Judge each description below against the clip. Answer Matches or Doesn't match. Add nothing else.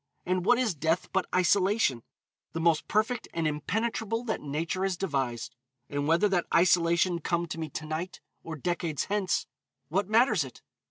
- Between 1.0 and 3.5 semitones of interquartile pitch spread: Doesn't match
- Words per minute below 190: Matches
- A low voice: Doesn't match